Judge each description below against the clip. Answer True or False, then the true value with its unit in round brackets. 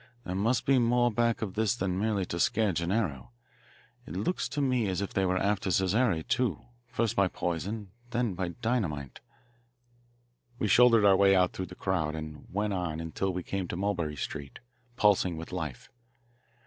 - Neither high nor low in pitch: False (95 Hz)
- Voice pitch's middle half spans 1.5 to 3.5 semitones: False (4.3 semitones)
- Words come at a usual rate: True (175 wpm)